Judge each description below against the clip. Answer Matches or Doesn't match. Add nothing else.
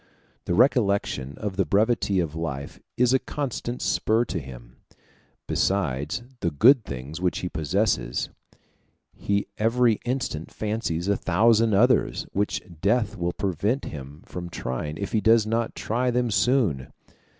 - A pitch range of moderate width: Doesn't match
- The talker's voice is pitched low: Matches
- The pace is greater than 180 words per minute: Doesn't match